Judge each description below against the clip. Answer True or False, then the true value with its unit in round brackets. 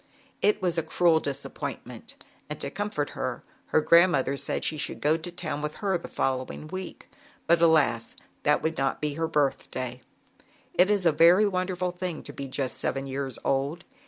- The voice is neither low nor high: True (160 Hz)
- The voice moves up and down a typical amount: True (4.3 semitones)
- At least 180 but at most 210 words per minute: True (185 wpm)